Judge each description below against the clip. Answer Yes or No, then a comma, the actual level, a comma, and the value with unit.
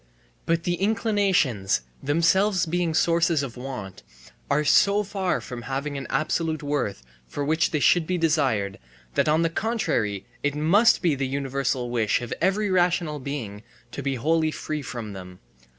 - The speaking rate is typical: Yes, average, 160 wpm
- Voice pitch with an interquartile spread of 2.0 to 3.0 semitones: No, average, 5.3 semitones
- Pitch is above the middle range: No, medium, 150 Hz